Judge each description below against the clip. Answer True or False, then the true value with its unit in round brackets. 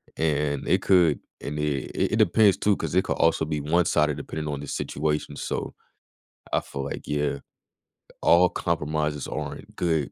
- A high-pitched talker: False (75 Hz)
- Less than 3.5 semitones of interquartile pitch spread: True (2.5 semitones)